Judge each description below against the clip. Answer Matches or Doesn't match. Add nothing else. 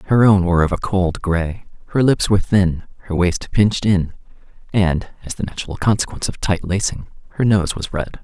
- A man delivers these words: Matches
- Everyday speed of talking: Matches